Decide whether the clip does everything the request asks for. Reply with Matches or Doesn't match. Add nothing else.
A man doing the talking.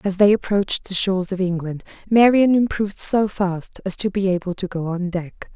Doesn't match